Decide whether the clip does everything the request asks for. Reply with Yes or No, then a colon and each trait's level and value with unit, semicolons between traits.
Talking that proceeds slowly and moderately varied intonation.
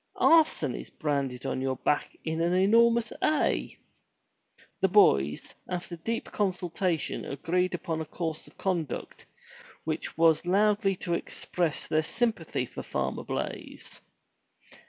Yes: slow, 125 wpm; average, 4.1 semitones